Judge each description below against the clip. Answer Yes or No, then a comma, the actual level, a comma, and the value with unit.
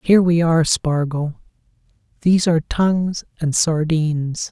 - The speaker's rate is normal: No, slow, 105 wpm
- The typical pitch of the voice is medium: Yes, medium, 160 Hz